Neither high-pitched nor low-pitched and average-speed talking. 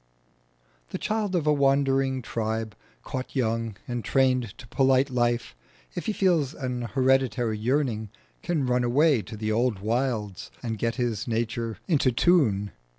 No: low, 125 Hz; average, 150 wpm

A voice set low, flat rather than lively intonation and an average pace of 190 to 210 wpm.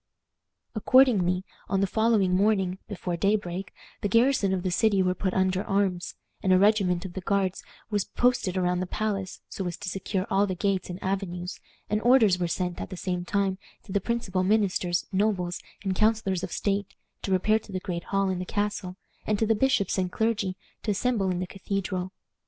No: high, 195 Hz; narrow, 2.2 semitones; average, 195 wpm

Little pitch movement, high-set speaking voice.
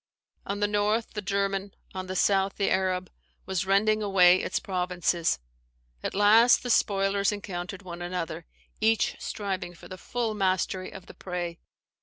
Yes: narrow, 2.1 semitones; high, 195 Hz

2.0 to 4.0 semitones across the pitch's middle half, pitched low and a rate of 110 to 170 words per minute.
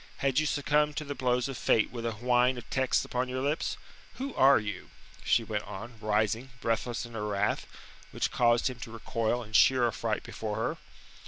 No: average, 2.9 semitones; low, 120 Hz; average, 195 wpm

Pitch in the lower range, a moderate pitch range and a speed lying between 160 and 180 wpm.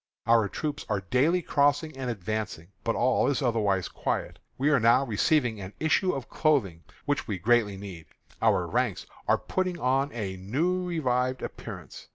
No: low, 125 Hz; wide, 5.9 semitones; average, 165 wpm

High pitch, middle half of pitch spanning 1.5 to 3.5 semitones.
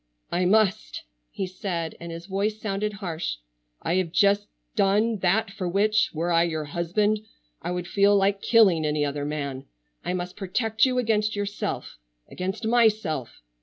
No: high, 195 Hz; average, 3.9 semitones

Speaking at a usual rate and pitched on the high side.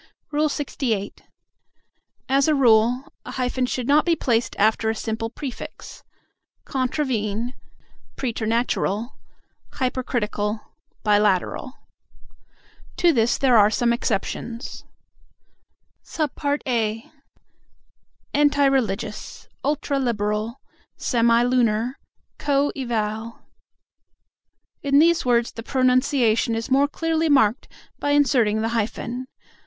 No: slow, 95 wpm; high, 240 Hz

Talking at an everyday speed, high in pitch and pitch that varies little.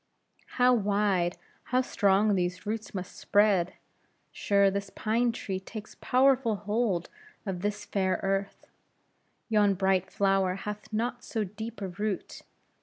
No: slow, 130 wpm; high, 205 Hz; narrow, 2.2 semitones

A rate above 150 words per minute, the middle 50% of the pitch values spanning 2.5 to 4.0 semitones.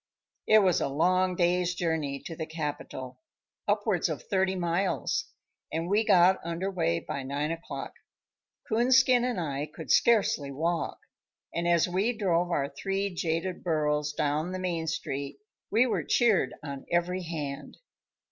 No: average, 145 wpm; average, 3.7 semitones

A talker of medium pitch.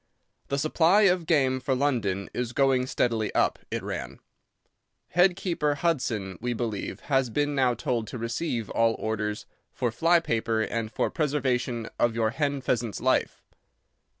No: low, 125 Hz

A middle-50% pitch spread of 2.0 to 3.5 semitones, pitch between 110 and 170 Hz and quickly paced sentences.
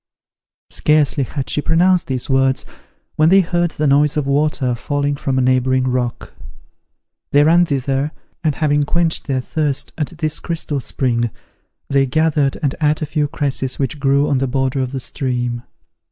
No: narrow, 2.6 semitones; medium, 140 Hz; average, 170 wpm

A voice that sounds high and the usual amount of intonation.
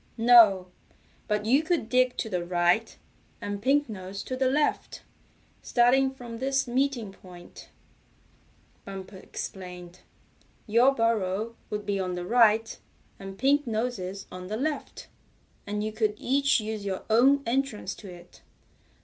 Yes: high, 220 Hz; average, 4.8 semitones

